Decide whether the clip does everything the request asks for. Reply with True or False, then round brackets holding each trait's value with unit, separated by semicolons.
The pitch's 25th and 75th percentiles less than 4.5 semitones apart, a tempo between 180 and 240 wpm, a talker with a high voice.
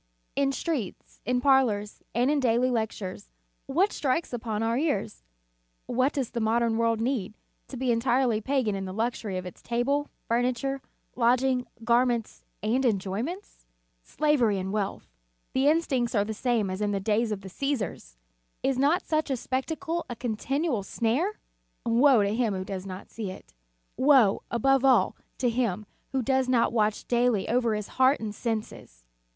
False (3.9 semitones; 165 wpm; 240 Hz)